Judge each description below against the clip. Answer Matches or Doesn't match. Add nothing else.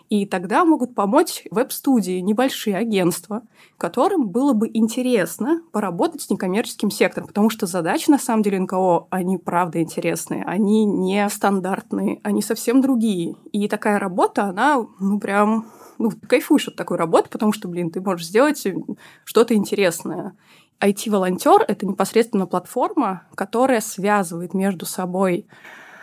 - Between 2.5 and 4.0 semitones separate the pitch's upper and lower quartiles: Matches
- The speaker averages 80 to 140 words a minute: Matches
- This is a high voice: Matches